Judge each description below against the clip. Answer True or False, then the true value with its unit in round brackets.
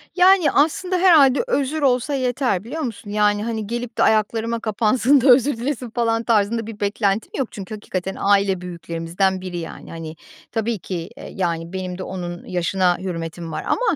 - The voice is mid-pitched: False (215 Hz)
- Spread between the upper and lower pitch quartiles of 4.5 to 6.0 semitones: True (5.3 semitones)